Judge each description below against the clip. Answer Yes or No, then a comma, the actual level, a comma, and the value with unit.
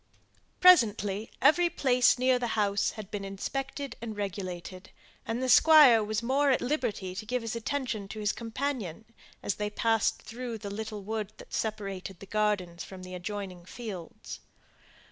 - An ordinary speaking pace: Yes, average, 160 wpm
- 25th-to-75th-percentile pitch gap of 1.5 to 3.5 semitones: No, average, 3.9 semitones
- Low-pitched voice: No, high, 215 Hz